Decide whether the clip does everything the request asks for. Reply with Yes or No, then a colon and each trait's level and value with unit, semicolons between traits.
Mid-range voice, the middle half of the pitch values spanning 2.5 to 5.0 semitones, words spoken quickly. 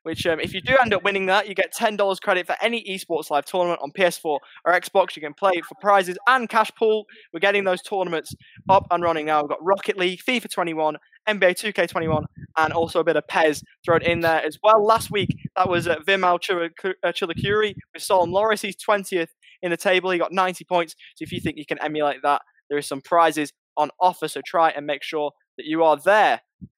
Yes: medium, 180 Hz; average, 3.5 semitones; fast, 220 wpm